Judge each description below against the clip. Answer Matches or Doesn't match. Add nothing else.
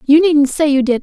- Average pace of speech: Doesn't match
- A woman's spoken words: Matches